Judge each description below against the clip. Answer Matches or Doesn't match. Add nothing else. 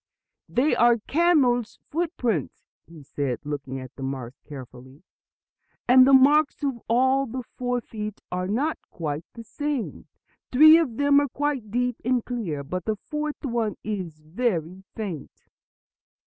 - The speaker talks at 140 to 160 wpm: Matches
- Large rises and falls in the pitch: Matches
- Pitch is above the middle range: Matches